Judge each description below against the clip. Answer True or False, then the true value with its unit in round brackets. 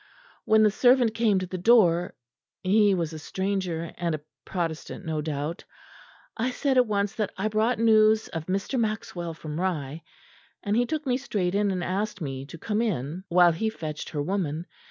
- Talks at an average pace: True (185 wpm)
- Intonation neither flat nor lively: True (4.7 semitones)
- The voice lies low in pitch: False (190 Hz)